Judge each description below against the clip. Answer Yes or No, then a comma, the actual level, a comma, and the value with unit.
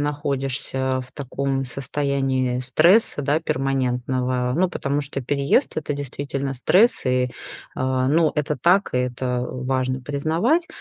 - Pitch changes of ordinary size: No, narrow, 2.2 semitones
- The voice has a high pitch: No, low, 135 Hz